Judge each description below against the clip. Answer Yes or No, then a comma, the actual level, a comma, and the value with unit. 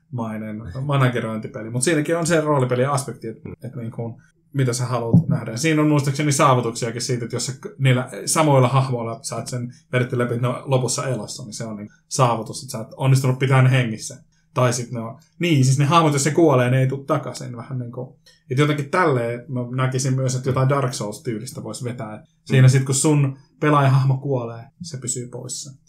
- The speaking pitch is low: Yes, low, 130 Hz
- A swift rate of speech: Yes, fast, 195 wpm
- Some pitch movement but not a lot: Yes, average, 3.1 semitones